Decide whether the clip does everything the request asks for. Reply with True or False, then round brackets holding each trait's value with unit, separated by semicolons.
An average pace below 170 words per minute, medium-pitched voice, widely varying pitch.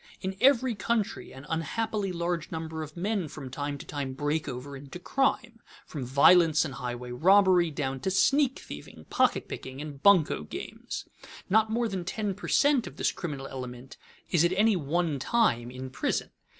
False (175 wpm; 165 Hz; 6.8 semitones)